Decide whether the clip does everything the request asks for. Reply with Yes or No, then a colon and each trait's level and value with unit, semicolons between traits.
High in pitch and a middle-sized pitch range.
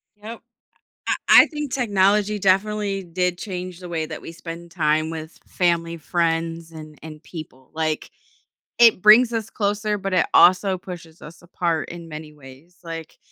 No: medium, 175 Hz; average, 3.5 semitones